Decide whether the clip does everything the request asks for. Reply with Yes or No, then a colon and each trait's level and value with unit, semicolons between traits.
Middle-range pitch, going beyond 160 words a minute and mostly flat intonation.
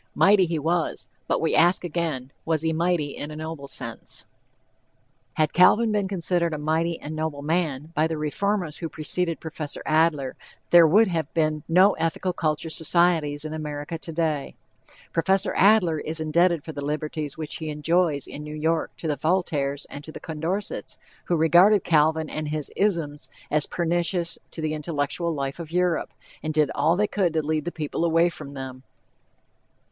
Yes: medium, 160 Hz; average, 170 wpm; narrow, 2.3 semitones